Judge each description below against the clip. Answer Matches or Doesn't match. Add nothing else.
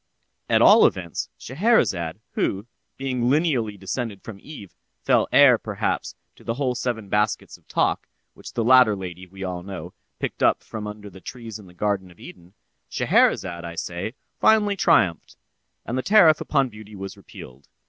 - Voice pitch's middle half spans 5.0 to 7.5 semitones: Matches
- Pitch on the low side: Matches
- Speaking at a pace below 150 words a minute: Doesn't match